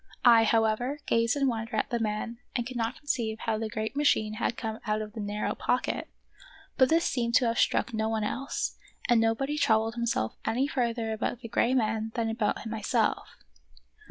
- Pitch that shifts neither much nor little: No, narrow, 2.0 semitones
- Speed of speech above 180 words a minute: Yes, average, 190 wpm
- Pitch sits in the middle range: No, high, 230 Hz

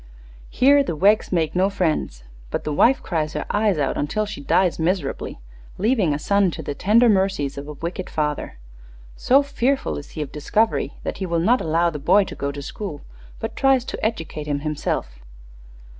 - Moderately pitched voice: Yes, medium, 175 Hz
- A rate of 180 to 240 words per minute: Yes, average, 190 wpm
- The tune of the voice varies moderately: No, wide, 6.0 semitones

